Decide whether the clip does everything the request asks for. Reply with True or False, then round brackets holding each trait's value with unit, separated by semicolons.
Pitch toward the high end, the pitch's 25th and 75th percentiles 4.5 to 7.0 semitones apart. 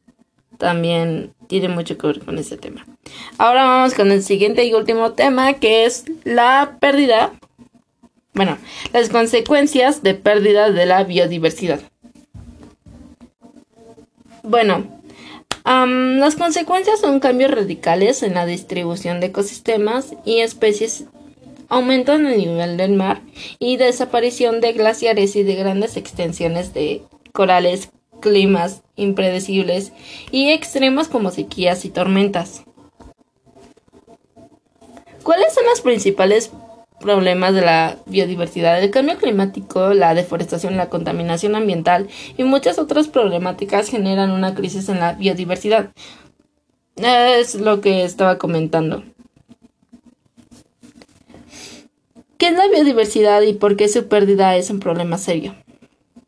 True (210 Hz; 4.9 semitones)